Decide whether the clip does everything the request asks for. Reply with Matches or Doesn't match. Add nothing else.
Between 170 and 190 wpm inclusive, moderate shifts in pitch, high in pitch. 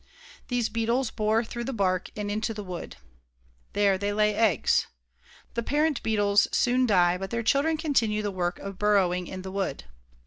Matches